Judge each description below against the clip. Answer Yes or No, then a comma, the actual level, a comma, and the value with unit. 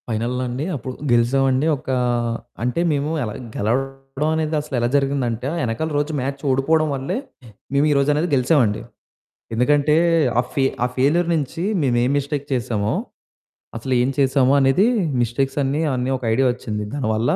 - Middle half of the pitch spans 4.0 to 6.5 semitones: No, average, 2.8 semitones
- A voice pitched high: No, low, 135 Hz